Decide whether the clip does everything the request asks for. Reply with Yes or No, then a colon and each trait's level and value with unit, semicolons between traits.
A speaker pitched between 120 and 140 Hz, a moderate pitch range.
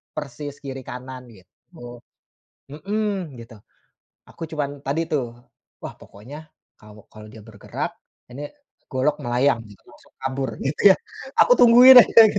Yes: low, 135 Hz; average, 4.3 semitones